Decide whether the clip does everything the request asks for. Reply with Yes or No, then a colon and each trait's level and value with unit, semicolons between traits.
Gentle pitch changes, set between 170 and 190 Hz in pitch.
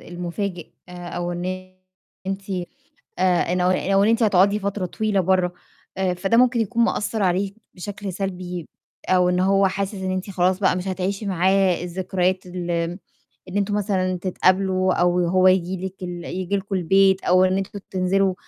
Yes: narrow, 1.5 semitones; medium, 185 Hz